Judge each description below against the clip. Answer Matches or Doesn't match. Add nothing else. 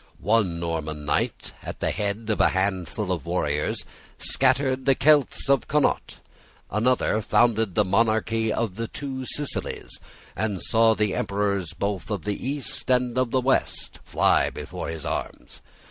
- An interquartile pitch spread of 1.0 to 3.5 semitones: Doesn't match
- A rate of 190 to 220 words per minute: Doesn't match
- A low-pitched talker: Matches